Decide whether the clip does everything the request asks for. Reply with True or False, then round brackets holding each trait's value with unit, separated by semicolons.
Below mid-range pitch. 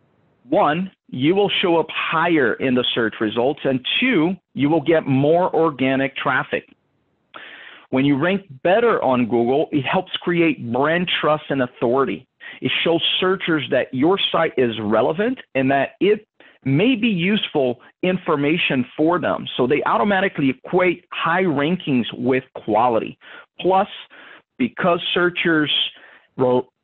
False (160 Hz)